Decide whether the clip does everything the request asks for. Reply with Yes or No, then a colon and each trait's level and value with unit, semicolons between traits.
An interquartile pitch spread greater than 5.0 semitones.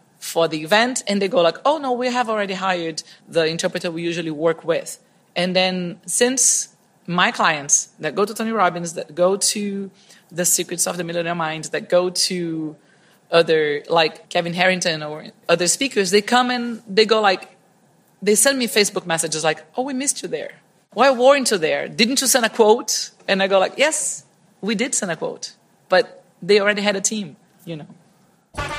No: average, 4.3 semitones